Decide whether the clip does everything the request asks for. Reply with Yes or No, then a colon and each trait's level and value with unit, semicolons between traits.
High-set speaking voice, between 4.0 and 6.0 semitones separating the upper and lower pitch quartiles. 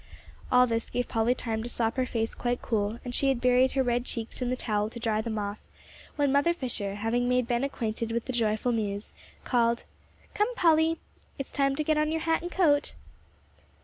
No: high, 245 Hz; average, 3.4 semitones